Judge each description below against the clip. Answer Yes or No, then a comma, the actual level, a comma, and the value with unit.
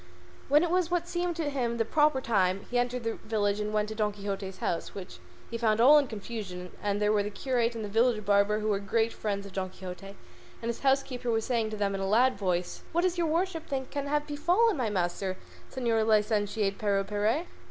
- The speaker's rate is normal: No, fast, 225 wpm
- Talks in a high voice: Yes, high, 220 Hz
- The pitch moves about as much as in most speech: Yes, average, 4.8 semitones